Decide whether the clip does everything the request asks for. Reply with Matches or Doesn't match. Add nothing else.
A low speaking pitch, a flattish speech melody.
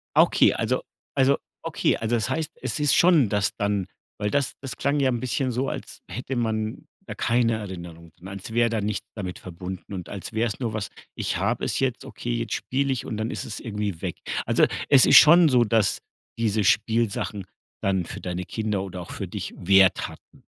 Doesn't match